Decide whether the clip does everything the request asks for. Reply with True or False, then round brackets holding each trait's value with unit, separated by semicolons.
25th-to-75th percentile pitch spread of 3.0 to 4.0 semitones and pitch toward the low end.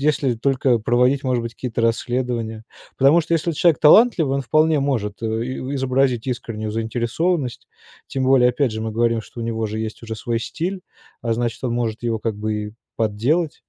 True (3.4 semitones; 120 Hz)